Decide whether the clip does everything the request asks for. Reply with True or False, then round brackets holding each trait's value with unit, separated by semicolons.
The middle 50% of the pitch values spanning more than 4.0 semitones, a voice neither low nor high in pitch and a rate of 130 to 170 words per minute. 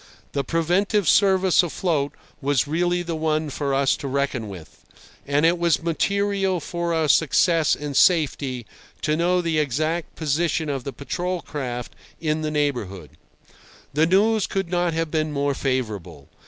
False (3.7 semitones; 155 Hz; 155 wpm)